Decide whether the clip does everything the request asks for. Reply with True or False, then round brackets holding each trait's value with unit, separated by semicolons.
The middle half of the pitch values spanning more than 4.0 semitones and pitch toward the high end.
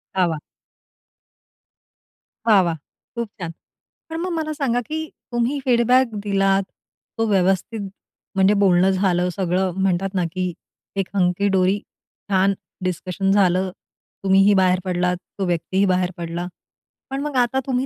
False (3.7 semitones; 195 Hz)